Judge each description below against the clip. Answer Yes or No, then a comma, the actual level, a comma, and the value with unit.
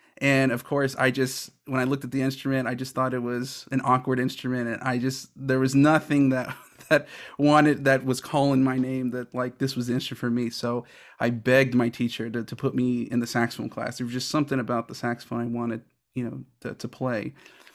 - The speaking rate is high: Yes, fast, 230 wpm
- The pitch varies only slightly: Yes, narrow, 1.7 semitones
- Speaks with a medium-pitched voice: No, low, 130 Hz